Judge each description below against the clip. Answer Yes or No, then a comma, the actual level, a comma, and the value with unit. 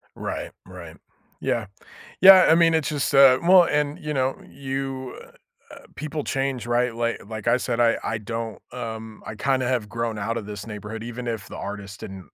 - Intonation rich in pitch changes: No, average, 3.8 semitones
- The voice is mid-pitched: No, low, 120 Hz